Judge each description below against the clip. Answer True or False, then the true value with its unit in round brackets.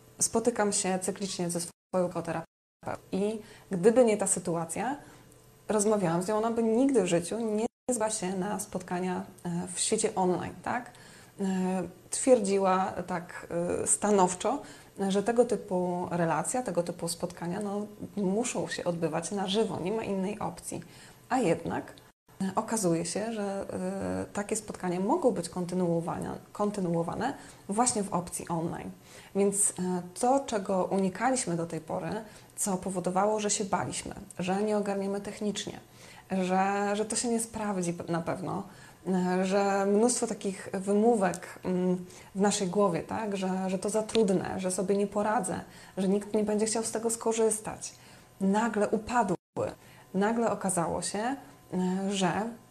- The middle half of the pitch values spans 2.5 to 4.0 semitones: True (3.0 semitones)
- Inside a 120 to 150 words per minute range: True (135 wpm)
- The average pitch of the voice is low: False (195 Hz)